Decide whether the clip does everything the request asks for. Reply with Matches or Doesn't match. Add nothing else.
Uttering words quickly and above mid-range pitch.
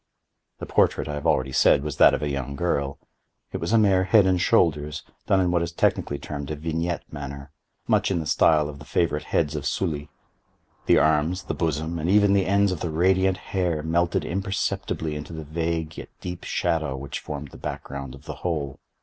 Doesn't match